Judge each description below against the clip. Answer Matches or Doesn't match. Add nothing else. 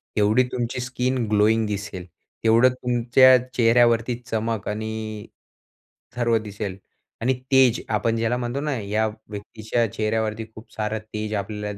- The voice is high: Doesn't match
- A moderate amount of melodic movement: Doesn't match